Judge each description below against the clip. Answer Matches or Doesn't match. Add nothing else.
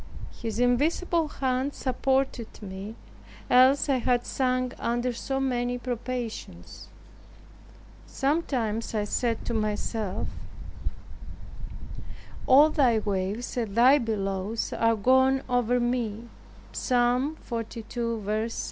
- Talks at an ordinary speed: Doesn't match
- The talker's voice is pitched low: Doesn't match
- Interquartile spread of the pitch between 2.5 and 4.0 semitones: Matches